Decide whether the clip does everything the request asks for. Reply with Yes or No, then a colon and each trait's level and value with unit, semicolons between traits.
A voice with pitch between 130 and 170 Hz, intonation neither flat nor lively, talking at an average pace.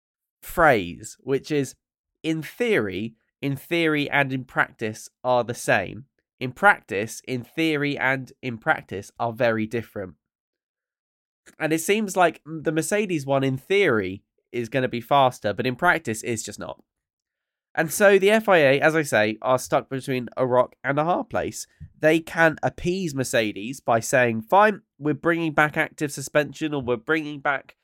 Yes: medium, 140 Hz; average, 4.8 semitones; average, 160 wpm